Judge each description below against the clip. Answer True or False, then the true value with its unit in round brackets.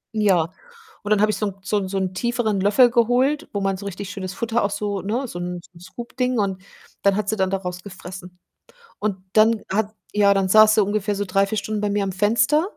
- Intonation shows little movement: True (2.2 semitones)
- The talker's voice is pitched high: True (205 Hz)